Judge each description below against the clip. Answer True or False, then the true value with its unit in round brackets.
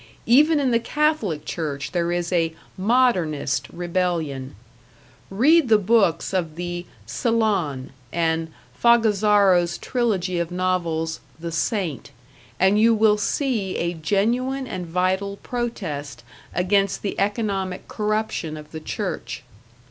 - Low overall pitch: False (185 Hz)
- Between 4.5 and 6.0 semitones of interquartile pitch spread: True (4.8 semitones)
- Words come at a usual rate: False (120 wpm)